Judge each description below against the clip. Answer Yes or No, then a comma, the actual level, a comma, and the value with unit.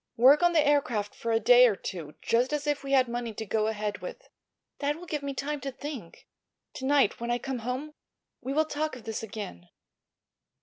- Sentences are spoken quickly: Yes, fast, 215 wpm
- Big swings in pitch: No, average, 4.5 semitones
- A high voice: Yes, very high, 255 Hz